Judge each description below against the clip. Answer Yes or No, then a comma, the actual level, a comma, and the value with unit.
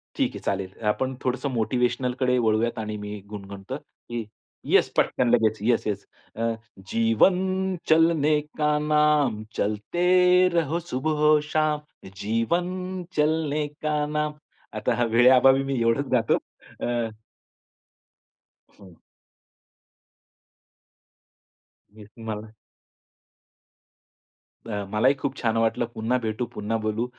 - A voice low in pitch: Yes, low, 125 Hz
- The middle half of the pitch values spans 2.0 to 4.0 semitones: No, wide, 5.4 semitones